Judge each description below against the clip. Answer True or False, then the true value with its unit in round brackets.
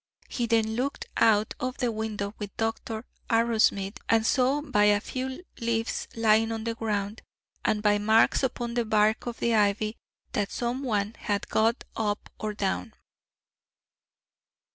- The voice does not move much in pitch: True (2.0 semitones)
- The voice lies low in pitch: False (225 Hz)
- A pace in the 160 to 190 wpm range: False (150 wpm)